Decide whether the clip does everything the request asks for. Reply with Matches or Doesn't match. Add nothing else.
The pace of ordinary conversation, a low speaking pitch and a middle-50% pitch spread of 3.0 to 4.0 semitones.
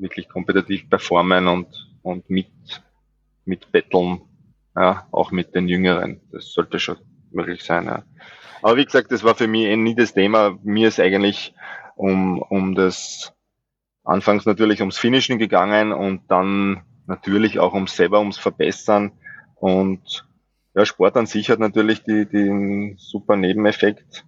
Doesn't match